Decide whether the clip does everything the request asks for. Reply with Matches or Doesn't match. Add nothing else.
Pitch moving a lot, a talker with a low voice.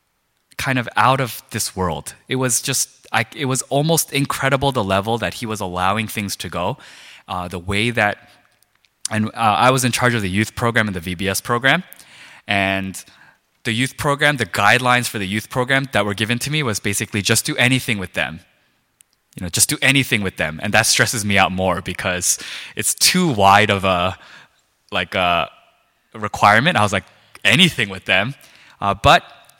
Doesn't match